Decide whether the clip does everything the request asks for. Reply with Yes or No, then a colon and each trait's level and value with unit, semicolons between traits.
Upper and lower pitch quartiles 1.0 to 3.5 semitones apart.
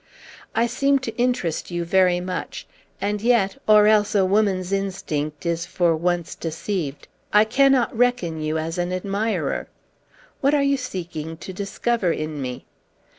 No: average, 4.9 semitones